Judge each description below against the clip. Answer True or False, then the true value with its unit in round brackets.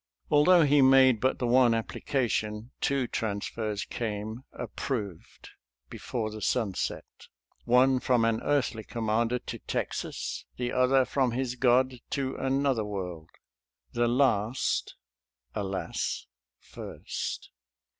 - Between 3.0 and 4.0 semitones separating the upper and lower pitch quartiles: True (3.4 semitones)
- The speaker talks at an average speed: False (130 wpm)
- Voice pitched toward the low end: True (120 Hz)